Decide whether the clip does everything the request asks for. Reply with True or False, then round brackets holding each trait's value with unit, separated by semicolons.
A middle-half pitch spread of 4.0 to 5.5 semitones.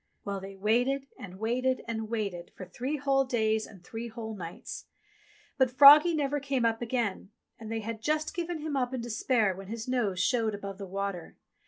True (4.6 semitones)